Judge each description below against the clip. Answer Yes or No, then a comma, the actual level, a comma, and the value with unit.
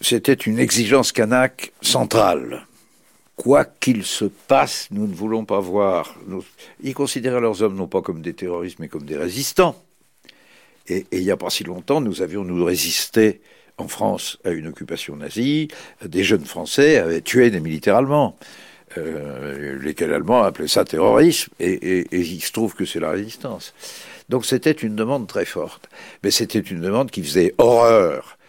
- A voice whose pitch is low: Yes, low, 110 Hz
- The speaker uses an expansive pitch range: Yes, wide, 6.5 semitones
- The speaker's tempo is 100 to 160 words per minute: No, average, 175 wpm